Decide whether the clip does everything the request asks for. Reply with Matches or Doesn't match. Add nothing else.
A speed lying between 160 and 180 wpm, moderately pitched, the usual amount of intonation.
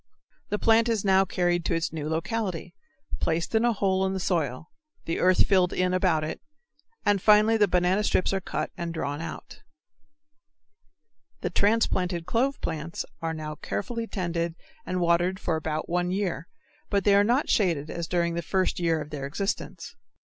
Matches